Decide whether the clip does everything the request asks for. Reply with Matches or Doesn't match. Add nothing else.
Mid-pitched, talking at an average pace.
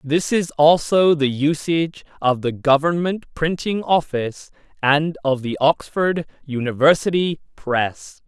Doesn't match